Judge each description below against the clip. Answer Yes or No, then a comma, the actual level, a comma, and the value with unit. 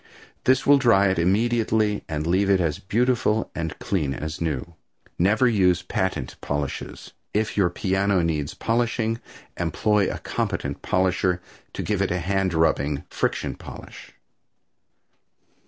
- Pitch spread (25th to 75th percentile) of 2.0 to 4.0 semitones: No, average, 4.6 semitones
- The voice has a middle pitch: No, very low, 95 Hz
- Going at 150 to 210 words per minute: No, slow, 135 wpm